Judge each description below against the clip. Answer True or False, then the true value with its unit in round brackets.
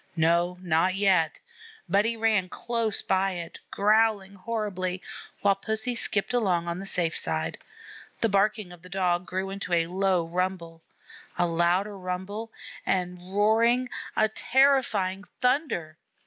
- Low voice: False (190 Hz)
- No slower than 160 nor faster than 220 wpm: False (135 wpm)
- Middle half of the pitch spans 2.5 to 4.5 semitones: True (3.5 semitones)